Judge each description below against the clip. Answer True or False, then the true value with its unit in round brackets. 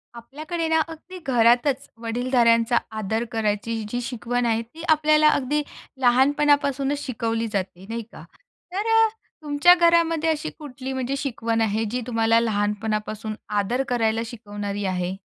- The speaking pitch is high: True (245 Hz)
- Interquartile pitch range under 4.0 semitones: False (4.5 semitones)